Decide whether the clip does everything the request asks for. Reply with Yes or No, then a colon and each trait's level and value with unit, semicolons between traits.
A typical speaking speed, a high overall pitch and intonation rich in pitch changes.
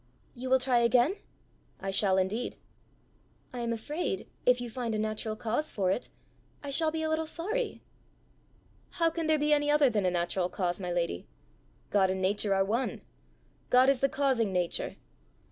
Yes: average, 180 wpm; high, 235 Hz; wide, 6.9 semitones